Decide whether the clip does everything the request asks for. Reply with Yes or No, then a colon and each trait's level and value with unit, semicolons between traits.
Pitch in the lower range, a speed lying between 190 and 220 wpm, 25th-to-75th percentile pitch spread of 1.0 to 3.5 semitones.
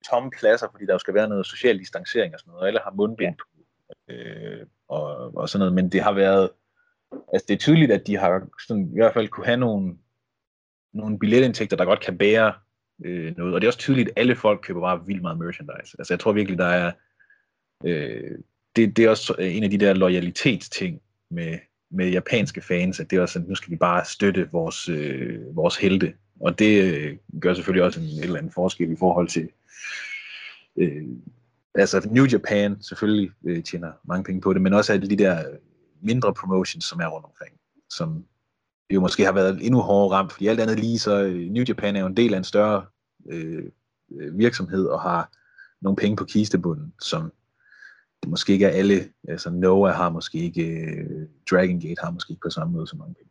Yes: low, 100 Hz; average, 210 wpm; average, 3.2 semitones